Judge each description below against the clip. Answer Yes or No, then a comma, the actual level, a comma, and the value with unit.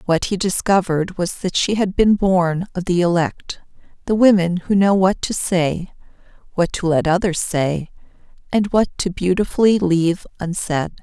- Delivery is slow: No, average, 160 wpm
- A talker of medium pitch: Yes, medium, 180 Hz